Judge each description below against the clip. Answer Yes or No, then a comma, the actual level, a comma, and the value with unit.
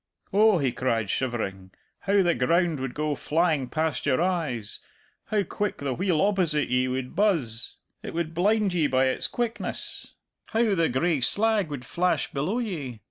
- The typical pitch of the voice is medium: Yes, medium, 160 Hz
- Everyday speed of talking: Yes, average, 165 wpm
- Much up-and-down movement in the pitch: Yes, wide, 6.6 semitones